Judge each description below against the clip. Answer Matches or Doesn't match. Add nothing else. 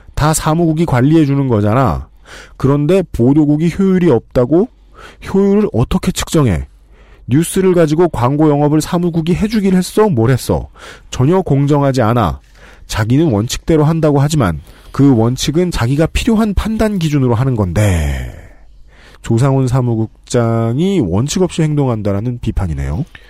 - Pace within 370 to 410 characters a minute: Doesn't match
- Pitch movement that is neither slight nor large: Doesn't match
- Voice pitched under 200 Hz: Matches